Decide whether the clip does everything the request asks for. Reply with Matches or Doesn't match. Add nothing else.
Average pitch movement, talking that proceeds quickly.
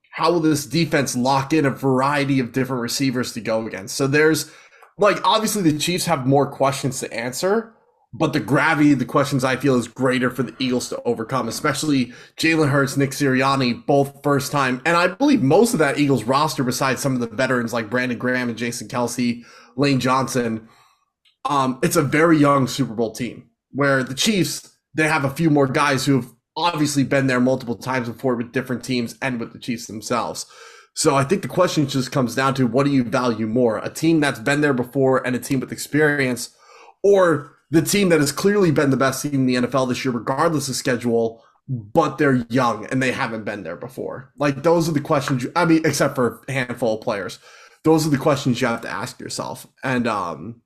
Matches